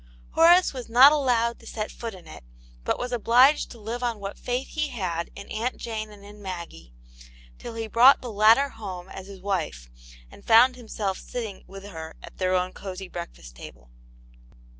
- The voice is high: Yes, high, 215 Hz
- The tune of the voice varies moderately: Yes, average, 4.7 semitones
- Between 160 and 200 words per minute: Yes, average, 185 wpm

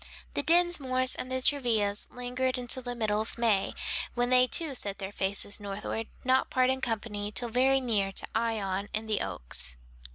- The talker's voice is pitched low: No, high, 235 Hz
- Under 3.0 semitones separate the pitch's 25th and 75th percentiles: No, average, 3.9 semitones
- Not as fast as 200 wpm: Yes, average, 165 wpm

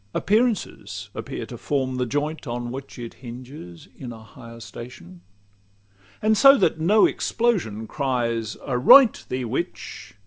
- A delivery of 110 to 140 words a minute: Yes, slow, 135 wpm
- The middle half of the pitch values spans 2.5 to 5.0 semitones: No, wide, 5.4 semitones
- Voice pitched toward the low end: Yes, low, 125 Hz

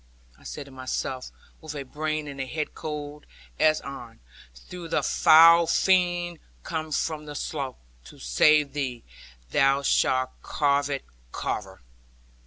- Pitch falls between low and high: Yes, medium, 145 Hz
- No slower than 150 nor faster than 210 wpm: No, slow, 135 wpm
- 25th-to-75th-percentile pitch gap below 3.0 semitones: Yes, narrow, 2.5 semitones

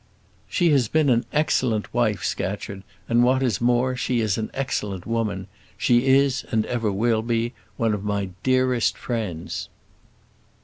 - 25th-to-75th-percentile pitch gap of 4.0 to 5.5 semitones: No, average, 3.2 semitones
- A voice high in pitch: No, low, 120 Hz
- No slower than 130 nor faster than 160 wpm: Yes, average, 150 wpm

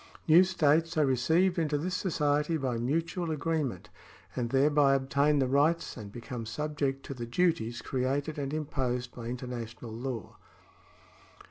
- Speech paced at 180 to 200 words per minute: No, average, 145 wpm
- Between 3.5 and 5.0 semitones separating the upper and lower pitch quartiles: Yes, average, 3.9 semitones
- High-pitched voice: No, medium, 140 Hz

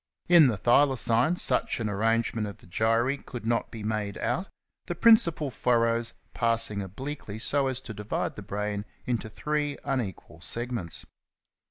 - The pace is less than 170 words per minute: Yes, average, 150 wpm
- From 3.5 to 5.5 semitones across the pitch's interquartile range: Yes, average, 4.0 semitones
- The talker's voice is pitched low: Yes, low, 115 Hz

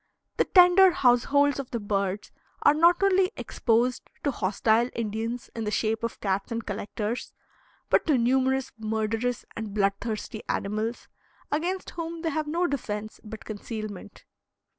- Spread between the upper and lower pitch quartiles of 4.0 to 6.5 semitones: Yes, average, 5.1 semitones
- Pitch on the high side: Yes, high, 230 Hz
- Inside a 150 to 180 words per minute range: No, average, 140 wpm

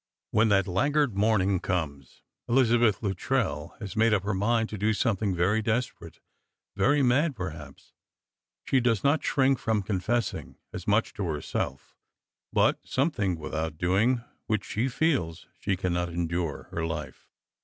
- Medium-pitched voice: No, low, 100 Hz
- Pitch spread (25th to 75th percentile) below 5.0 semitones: No, average, 5.3 semitones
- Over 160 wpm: No, average, 145 wpm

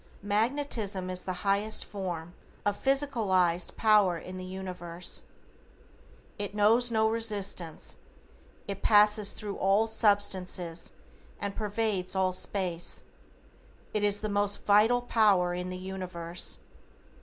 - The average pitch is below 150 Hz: No, high, 200 Hz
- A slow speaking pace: Yes, slow, 115 wpm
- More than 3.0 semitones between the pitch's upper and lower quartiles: No, average, 2.7 semitones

